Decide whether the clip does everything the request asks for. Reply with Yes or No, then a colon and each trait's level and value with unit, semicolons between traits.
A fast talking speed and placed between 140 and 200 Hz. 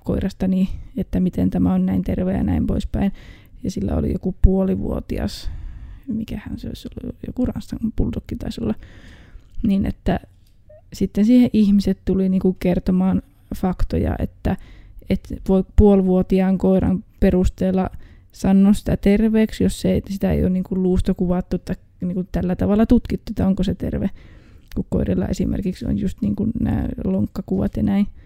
No: average, 145 wpm; high, 190 Hz